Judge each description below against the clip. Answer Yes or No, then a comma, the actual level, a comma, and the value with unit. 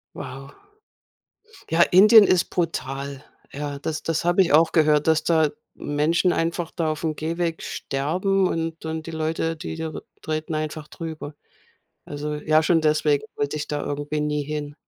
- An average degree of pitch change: No, narrow, 1.8 semitones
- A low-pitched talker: No, medium, 155 Hz